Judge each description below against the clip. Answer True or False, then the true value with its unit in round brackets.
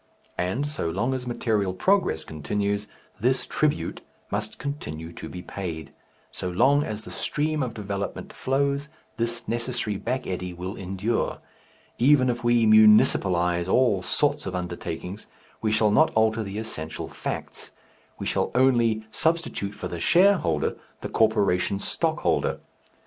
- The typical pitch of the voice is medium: False (110 Hz)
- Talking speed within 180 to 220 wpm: False (140 wpm)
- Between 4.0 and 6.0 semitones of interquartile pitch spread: True (5.4 semitones)